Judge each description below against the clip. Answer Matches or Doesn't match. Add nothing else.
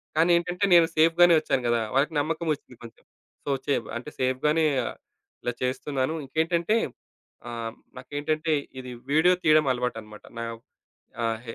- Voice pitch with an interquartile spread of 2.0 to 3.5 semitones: Doesn't match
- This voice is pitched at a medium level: Matches